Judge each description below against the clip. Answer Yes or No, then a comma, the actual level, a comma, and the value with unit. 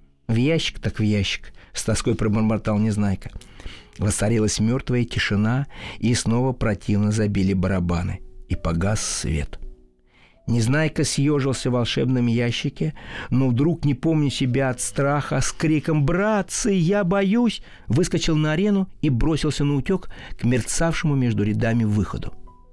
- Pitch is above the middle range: No, low, 120 Hz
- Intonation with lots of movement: Yes, wide, 6.2 semitones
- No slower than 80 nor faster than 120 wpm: No, average, 130 wpm